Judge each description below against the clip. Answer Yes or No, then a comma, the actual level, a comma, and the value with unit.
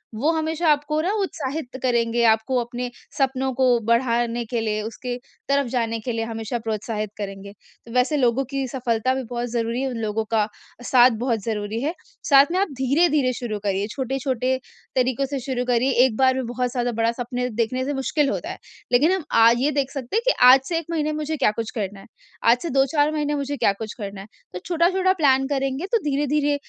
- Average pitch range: Yes, average, 3.5 semitones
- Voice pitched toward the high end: Yes, very high, 255 Hz